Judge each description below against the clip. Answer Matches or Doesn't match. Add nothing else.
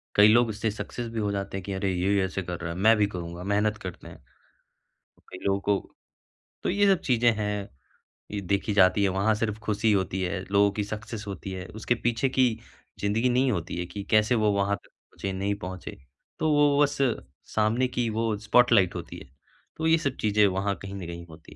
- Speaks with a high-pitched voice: Doesn't match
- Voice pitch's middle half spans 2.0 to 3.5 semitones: Matches